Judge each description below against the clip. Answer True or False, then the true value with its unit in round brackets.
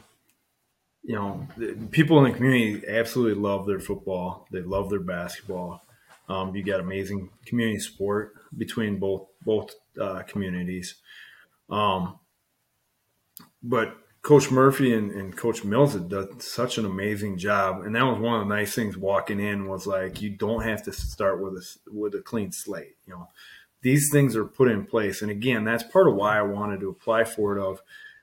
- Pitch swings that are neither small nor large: True (3.0 semitones)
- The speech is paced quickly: False (175 wpm)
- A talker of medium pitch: False (105 Hz)